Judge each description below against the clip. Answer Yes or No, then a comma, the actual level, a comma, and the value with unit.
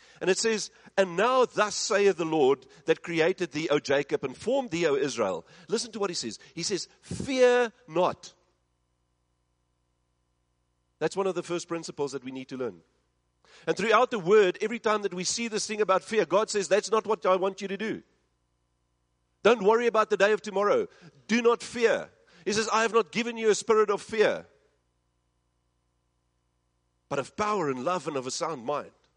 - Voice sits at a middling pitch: Yes, medium, 180 Hz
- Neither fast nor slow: Yes, average, 190 wpm